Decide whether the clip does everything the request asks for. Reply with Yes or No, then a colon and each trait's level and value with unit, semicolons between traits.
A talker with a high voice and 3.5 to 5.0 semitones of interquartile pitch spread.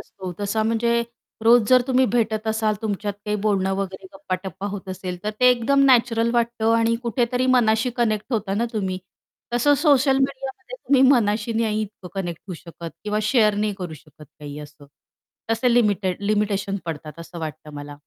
Yes: high, 215 Hz; average, 3.8 semitones